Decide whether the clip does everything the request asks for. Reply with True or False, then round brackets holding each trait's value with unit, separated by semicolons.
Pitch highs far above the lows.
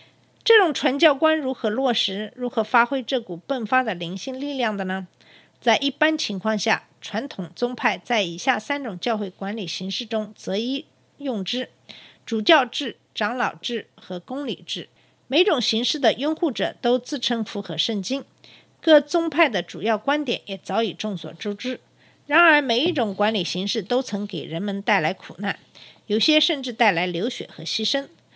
False (5.0 semitones)